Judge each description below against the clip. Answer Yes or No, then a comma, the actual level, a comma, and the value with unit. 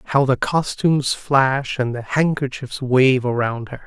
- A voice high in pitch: No, low, 130 Hz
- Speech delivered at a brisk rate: No, average, 155 wpm